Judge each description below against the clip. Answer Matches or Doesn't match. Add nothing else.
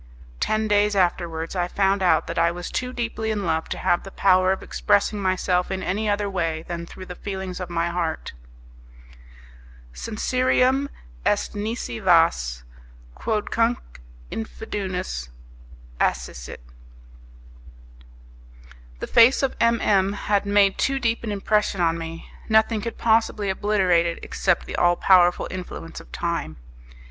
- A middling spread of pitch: Matches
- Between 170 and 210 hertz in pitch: Matches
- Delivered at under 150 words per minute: Matches